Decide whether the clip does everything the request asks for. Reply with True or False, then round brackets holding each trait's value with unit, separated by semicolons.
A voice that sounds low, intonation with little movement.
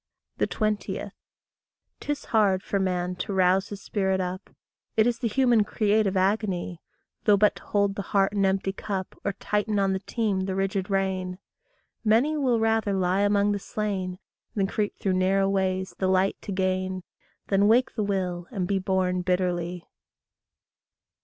False (195 Hz; 1.8 semitones)